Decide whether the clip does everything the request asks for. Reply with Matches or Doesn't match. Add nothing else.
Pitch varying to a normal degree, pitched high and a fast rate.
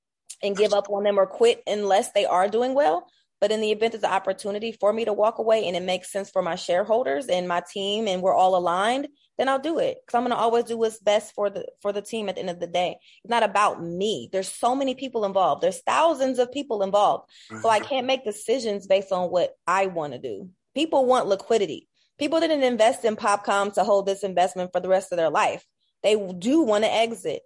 Matches